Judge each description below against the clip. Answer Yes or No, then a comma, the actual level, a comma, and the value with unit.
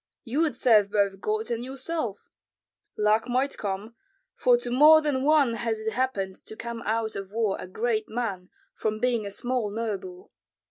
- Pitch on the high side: Yes, high, 230 Hz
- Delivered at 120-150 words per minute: No, average, 175 wpm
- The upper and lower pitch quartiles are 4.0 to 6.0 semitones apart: No, average, 3.3 semitones